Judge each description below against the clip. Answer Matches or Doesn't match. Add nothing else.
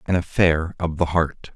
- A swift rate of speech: Doesn't match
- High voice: Doesn't match